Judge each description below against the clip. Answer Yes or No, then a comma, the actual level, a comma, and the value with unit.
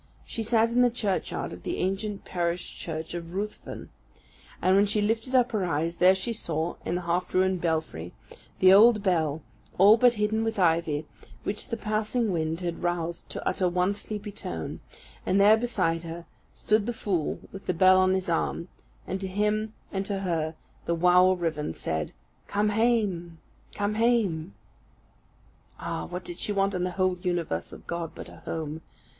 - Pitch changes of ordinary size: Yes, average, 3.7 semitones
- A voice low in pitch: No, medium, 185 Hz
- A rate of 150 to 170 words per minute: No, average, 180 wpm